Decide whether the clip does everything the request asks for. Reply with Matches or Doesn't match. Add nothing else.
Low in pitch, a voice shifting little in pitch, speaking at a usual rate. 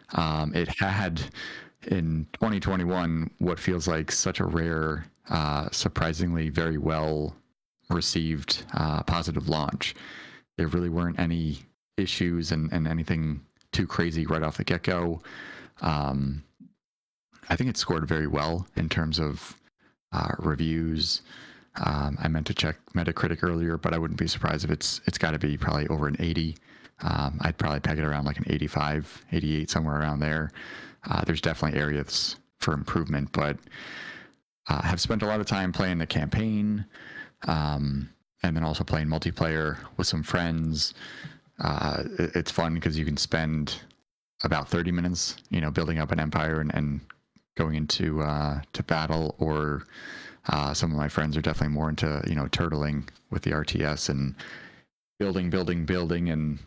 Matches